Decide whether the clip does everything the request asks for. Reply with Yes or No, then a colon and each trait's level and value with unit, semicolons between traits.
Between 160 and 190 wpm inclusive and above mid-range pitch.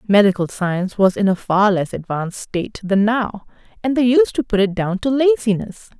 No: average, 200 wpm; high, 210 Hz